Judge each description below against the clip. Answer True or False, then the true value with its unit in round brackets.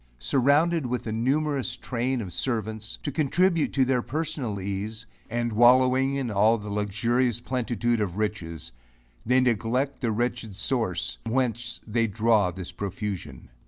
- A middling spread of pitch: True (3.7 semitones)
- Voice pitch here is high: False (120 Hz)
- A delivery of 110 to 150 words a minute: True (140 wpm)